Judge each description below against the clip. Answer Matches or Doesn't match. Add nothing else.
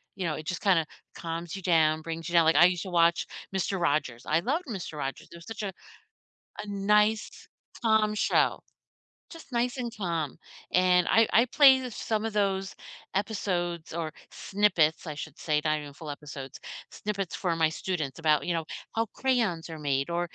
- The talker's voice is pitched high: Doesn't match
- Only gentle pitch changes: Doesn't match